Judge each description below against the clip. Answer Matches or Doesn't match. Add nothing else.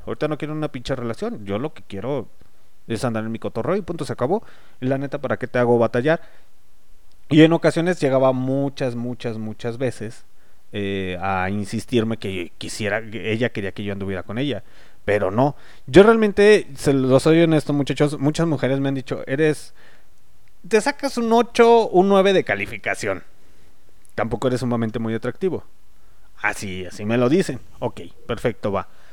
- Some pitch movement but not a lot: Doesn't match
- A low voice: Matches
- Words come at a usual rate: Matches